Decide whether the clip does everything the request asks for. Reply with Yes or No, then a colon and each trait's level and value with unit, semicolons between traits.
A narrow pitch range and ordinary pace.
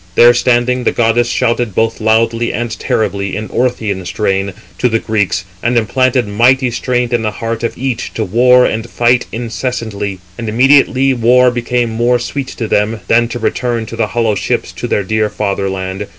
Yes: narrow, 2.2 semitones; average, 180 wpm